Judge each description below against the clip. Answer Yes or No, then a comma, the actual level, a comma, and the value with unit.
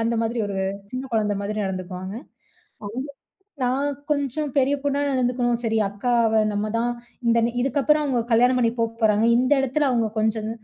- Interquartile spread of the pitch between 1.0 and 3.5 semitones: Yes, average, 3.1 semitones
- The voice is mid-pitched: No, high, 235 Hz